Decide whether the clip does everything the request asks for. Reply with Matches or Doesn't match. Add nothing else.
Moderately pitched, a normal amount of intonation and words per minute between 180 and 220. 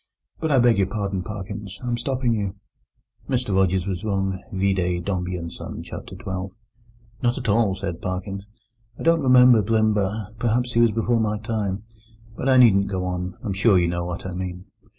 Doesn't match